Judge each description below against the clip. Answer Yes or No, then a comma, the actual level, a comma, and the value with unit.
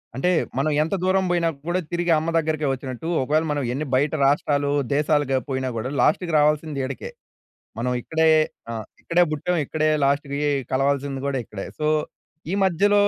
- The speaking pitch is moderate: Yes, medium, 150 Hz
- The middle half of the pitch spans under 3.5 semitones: Yes, average, 3.1 semitones